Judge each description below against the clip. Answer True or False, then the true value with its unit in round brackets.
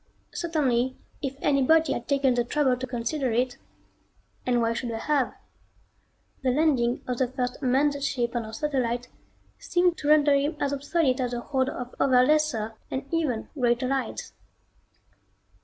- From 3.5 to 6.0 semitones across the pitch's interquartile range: False (3.0 semitones)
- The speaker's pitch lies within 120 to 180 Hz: False (260 Hz)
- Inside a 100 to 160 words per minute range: True (155 wpm)